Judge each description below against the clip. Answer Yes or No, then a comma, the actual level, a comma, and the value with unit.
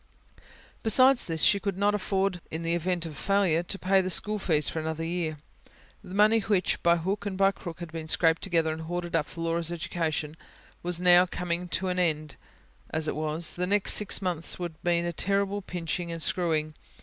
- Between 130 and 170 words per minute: No, fast, 205 wpm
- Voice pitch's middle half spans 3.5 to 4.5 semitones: No, average, 2.8 semitones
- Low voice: No, medium, 175 Hz